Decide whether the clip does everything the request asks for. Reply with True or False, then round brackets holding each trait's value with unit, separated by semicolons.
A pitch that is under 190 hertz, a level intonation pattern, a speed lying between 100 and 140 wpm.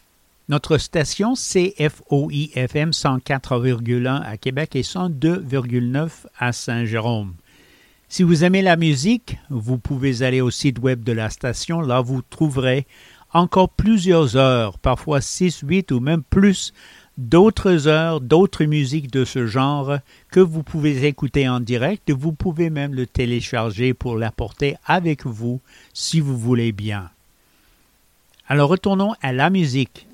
False (140 Hz; 4.8 semitones; 135 wpm)